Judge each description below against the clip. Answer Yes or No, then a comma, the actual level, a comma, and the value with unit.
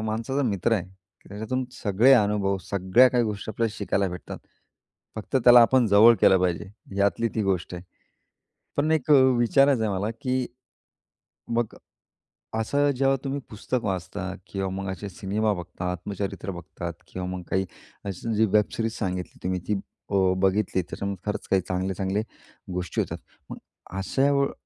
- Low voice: Yes, low, 105 Hz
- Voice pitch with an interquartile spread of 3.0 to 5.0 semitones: Yes, average, 3.8 semitones